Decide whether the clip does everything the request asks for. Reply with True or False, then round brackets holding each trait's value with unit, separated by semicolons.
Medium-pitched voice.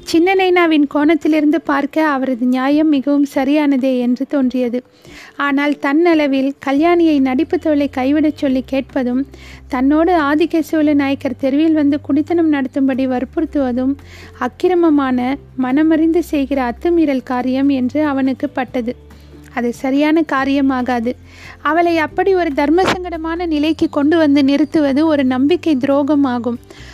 False (285 Hz)